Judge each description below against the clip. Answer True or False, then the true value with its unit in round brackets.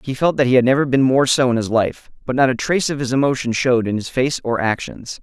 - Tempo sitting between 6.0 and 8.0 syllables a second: True (6.2 syllables/s)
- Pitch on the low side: True (130 Hz)